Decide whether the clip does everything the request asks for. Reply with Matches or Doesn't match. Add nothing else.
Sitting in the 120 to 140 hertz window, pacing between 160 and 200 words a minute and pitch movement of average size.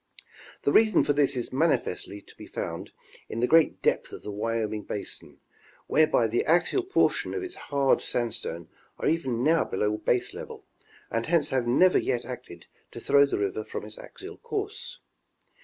Doesn't match